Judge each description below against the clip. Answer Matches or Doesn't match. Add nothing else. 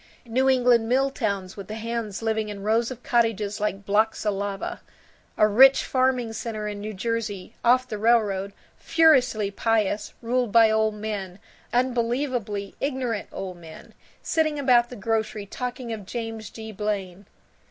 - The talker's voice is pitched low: Doesn't match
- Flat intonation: Doesn't match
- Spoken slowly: Doesn't match